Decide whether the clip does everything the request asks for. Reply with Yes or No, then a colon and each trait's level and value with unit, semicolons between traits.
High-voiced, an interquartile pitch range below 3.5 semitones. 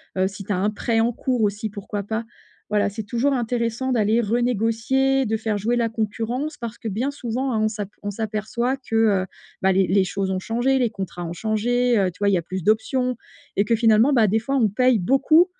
Yes: high, 225 Hz; average, 3.1 semitones